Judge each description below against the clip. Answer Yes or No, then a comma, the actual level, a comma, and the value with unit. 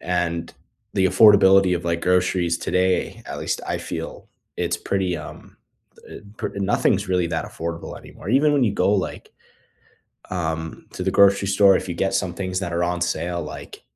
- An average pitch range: No, narrow, 2.2 semitones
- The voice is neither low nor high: No, very low, 90 Hz